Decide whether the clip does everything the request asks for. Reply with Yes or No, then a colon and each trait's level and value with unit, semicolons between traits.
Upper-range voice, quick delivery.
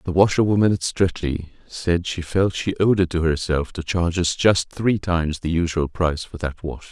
No: very low, 85 Hz; fast, 210 wpm